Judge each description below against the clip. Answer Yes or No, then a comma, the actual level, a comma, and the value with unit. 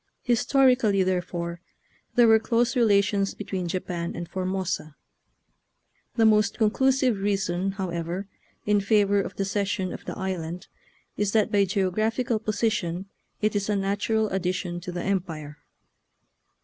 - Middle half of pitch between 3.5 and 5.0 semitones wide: No, average, 2.9 semitones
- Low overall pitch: No, high, 195 Hz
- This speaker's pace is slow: Yes, slow, 130 wpm